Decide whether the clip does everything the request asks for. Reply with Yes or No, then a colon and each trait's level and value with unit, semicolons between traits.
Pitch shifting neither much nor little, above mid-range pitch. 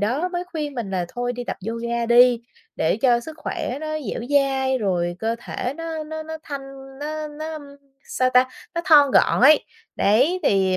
Yes: average, 4.6 semitones; very high, 265 Hz